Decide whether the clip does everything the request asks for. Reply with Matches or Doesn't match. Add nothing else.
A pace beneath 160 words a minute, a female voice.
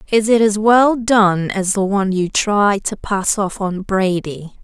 Doesn't match